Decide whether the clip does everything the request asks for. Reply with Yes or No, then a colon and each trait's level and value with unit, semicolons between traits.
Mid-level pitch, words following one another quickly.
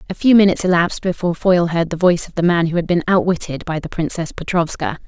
Yes: medium, 175 Hz; fast, 235 wpm